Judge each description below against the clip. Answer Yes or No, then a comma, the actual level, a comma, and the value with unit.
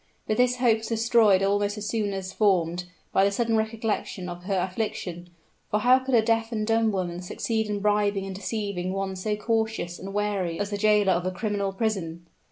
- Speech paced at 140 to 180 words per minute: No, average, 200 wpm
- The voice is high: Yes, high, 205 Hz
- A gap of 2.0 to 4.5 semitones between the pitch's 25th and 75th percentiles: Yes, average, 2.8 semitones